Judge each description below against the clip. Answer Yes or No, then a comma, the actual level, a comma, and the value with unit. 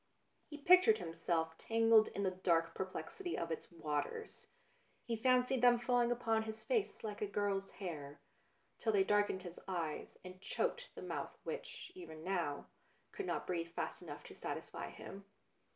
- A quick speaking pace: No, average, 160 wpm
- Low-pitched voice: No, high, 200 Hz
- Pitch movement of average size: No, wide, 6.2 semitones